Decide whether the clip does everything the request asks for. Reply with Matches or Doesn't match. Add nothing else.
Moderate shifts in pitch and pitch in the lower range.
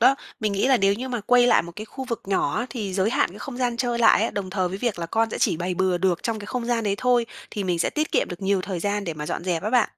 Doesn't match